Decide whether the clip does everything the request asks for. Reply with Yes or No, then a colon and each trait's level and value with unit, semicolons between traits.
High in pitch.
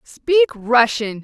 Yes: very high, 260 Hz